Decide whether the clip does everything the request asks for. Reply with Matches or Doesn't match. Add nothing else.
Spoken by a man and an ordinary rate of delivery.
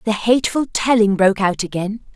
Doesn't match